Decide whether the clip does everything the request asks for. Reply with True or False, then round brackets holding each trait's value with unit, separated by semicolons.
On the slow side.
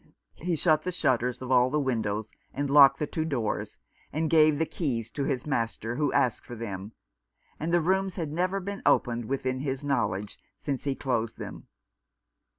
False (180 wpm)